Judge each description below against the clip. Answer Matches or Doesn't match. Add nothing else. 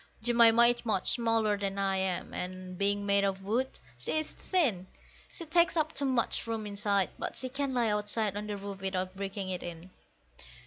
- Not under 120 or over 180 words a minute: Doesn't match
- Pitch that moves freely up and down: Doesn't match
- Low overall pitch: Doesn't match